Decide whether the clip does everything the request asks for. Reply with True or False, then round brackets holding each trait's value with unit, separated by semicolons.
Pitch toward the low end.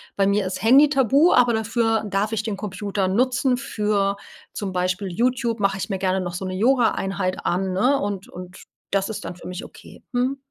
False (205 Hz)